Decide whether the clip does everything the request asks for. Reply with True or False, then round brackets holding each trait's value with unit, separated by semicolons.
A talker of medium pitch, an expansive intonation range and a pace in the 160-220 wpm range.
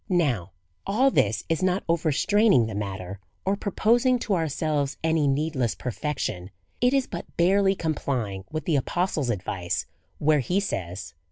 False (155 Hz; 8.3 semitones; 145 wpm)